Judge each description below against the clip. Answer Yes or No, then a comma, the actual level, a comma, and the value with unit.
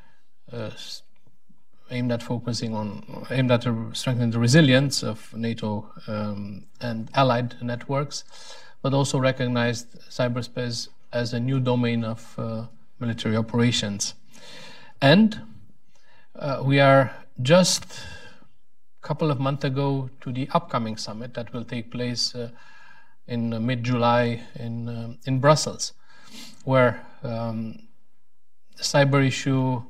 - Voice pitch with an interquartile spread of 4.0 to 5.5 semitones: No, average, 2.9 semitones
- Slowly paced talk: Yes, slow, 120 wpm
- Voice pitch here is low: Yes, low, 125 Hz